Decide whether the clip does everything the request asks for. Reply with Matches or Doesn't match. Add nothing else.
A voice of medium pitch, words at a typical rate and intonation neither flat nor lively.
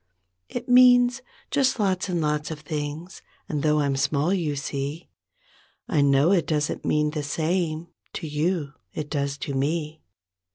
Matches